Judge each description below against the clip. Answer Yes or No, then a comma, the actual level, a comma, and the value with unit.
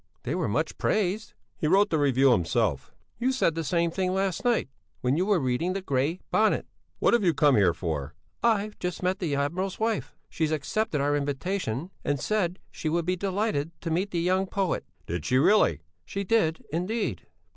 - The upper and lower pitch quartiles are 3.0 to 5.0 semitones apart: No, wide, 5.5 semitones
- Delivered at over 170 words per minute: Yes, average, 190 wpm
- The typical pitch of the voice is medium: Yes, medium, 170 Hz